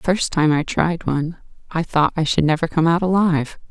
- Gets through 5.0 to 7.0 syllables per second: Yes, 5.5 syllables/s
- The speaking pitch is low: No, medium, 165 Hz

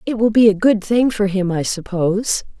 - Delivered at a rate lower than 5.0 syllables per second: No, 5.1 syllables/s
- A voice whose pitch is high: Yes, high, 205 Hz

